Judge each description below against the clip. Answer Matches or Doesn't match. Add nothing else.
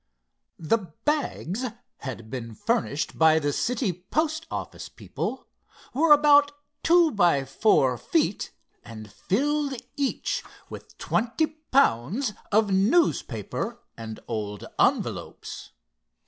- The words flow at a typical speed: Doesn't match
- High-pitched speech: Matches